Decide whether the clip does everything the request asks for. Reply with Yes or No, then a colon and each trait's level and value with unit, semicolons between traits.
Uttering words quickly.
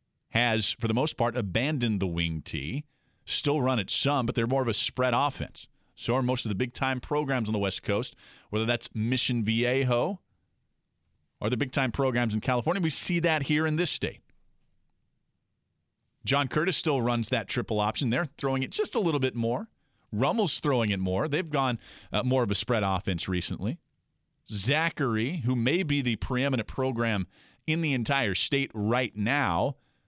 No: average, 180 wpm